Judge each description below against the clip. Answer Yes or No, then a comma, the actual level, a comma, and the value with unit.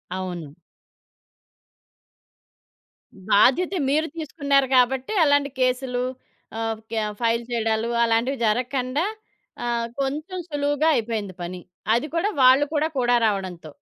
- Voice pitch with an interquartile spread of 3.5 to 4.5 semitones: Yes, average, 4.2 semitones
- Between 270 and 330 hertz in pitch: No, very high, 250 Hz